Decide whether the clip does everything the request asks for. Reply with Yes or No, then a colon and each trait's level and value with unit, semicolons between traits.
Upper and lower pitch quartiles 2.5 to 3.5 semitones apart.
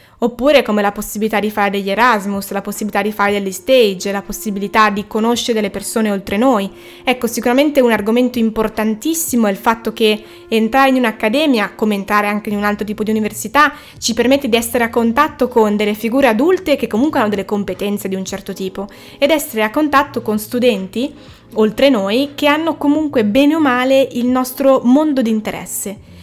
No: average, 4.2 semitones